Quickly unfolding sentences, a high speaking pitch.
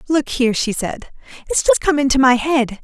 Yes: fast, 210 wpm; very high, 275 Hz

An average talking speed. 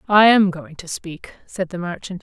No: fast, 215 wpm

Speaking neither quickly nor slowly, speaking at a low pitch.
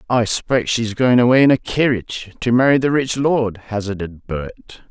Yes: average, 185 wpm; low, 115 Hz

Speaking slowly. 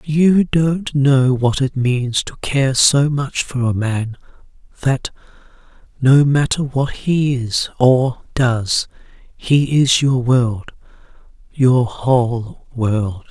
Yes: slow, 125 wpm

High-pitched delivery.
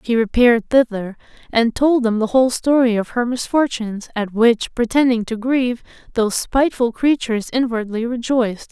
Yes: high, 235 Hz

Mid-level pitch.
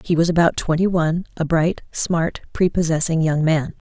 Yes: medium, 165 Hz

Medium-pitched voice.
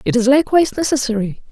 No: very high, 265 Hz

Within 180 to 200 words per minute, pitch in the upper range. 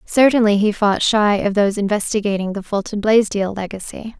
No: average, 155 wpm; high, 205 Hz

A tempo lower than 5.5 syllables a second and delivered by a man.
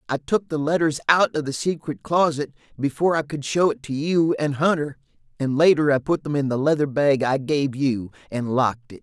Yes: 5.3 syllables/s; male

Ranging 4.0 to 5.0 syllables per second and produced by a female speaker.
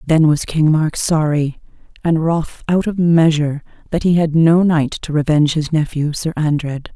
Yes: 4.6 syllables/s; female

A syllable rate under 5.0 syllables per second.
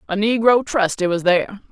No: 5.5 syllables/s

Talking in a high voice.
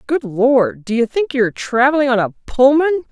Yes: very high, 260 Hz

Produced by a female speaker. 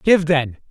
No: male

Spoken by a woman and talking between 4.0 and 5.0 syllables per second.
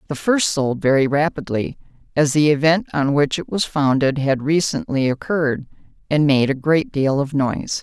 Yes: female; 4.8 syllables/s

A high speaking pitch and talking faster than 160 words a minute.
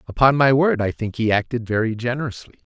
No: low, 120 Hz; average, 200 wpm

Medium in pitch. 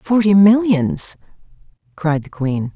Yes: medium, 175 Hz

